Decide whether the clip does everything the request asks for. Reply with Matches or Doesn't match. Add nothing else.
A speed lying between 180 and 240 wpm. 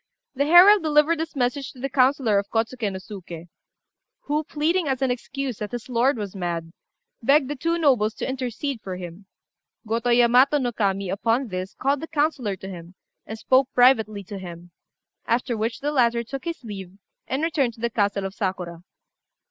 Matches